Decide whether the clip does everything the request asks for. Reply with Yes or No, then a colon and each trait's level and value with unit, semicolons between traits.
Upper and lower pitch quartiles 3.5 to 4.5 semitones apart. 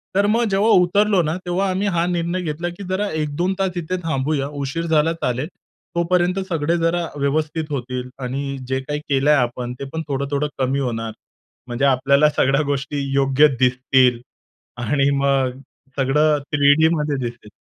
Yes: average, 4.2 semitones